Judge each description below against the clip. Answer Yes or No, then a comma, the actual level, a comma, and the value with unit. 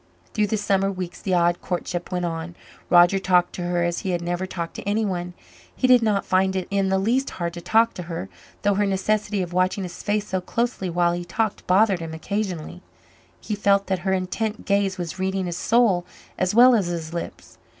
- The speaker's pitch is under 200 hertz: Yes, high, 190 Hz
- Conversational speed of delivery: No, fast, 210 wpm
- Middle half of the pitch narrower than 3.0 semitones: Yes, narrow, 2.6 semitones